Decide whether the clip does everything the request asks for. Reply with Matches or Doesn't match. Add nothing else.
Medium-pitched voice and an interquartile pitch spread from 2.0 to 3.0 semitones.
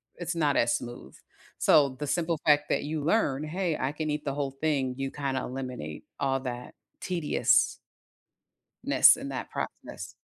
Matches